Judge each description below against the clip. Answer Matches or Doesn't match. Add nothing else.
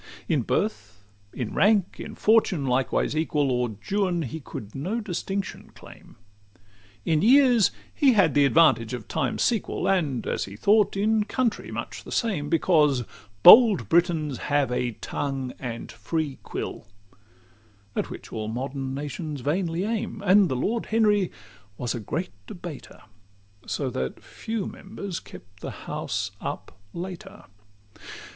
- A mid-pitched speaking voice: Matches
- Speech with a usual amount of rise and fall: Doesn't match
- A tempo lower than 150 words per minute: Matches